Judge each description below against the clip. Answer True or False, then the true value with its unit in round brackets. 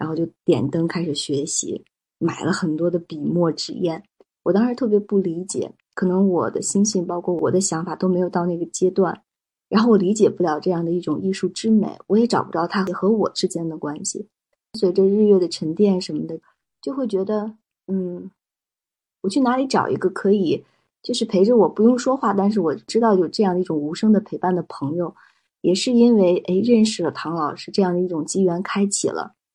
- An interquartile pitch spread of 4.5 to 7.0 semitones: False (3.2 semitones)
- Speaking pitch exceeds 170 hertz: True (185 Hz)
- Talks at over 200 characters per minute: True (300 characters per minute)